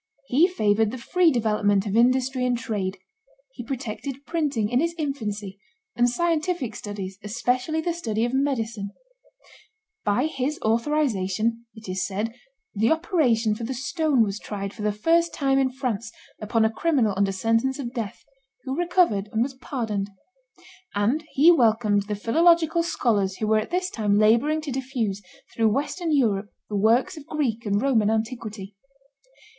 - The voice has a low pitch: No, high, 235 Hz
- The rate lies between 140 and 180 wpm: Yes, average, 160 wpm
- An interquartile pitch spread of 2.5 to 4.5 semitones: No, average, 5.0 semitones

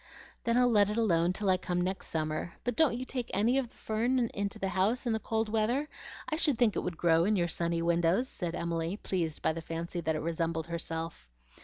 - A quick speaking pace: Yes, fast, 230 wpm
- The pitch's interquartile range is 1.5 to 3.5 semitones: No, average, 5.3 semitones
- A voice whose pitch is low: No, medium, 185 Hz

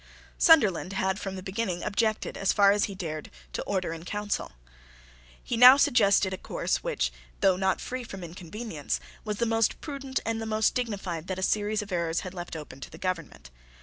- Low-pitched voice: No, high, 195 Hz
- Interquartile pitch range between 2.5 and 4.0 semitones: Yes, average, 3.7 semitones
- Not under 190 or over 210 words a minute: Yes, average, 200 wpm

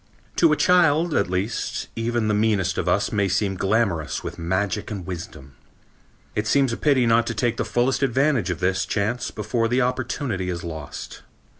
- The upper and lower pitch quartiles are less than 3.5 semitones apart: No, average, 4.8 semitones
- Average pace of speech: Yes, average, 180 wpm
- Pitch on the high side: No, low, 110 Hz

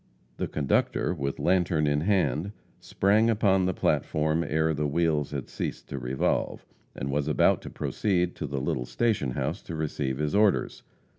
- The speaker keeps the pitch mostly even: No, average, 4.5 semitones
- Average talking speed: Yes, average, 165 wpm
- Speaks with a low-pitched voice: Yes, very low, 80 Hz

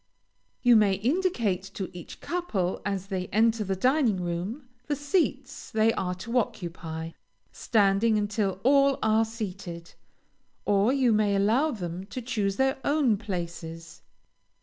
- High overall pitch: Yes, high, 210 Hz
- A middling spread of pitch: Yes, average, 4.8 semitones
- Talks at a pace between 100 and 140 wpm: Yes, slow, 135 wpm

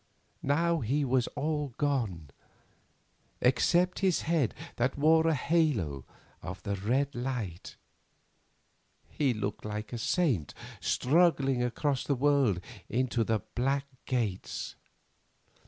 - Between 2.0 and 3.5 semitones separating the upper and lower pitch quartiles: No, average, 5.1 semitones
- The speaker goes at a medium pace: No, slow, 110 wpm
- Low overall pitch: Yes, low, 130 Hz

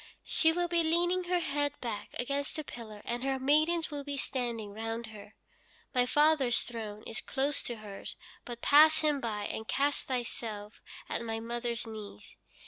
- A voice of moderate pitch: No, high, 245 Hz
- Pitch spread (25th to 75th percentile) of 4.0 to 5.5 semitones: Yes, average, 4.7 semitones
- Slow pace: No, average, 170 wpm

